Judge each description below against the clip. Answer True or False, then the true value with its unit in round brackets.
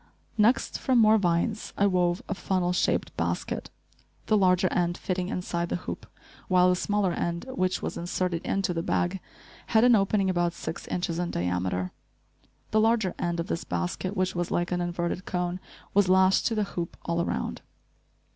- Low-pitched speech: False (180 Hz)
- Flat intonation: True (2.2 semitones)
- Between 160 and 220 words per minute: True (175 wpm)